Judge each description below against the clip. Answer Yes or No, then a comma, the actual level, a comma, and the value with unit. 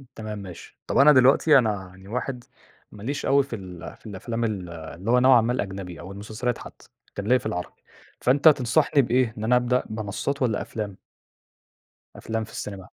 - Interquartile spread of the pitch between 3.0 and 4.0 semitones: No, average, 4.4 semitones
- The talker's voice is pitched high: No, low, 110 Hz